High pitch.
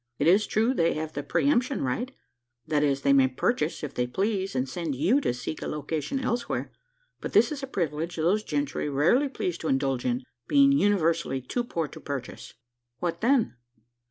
No: medium, 165 Hz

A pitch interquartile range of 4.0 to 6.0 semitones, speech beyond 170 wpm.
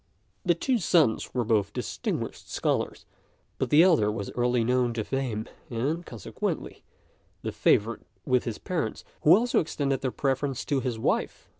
No: average, 4.8 semitones; average, 155 wpm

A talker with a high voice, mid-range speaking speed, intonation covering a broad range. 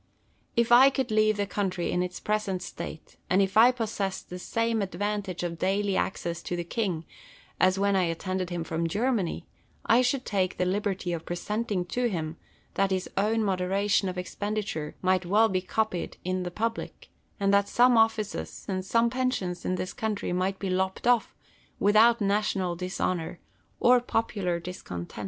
No: high, 195 Hz; average, 175 wpm; average, 3.2 semitones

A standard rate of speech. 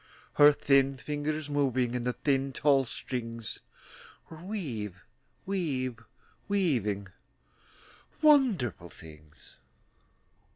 No: slow, 85 wpm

